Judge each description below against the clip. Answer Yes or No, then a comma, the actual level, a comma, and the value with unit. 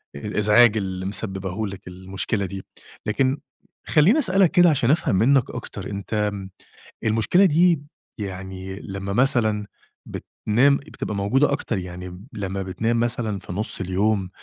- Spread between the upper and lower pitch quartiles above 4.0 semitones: Yes, average, 4.5 semitones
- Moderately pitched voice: No, low, 105 Hz